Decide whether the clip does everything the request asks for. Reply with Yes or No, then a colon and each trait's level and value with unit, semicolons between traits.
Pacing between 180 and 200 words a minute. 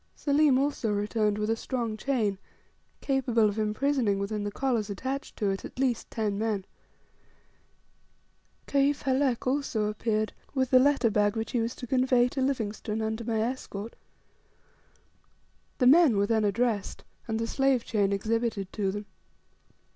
No: average, 150 wpm